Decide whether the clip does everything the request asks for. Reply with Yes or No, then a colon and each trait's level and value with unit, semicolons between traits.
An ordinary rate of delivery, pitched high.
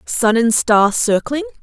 Yes: average, 150 wpm; very high, 250 Hz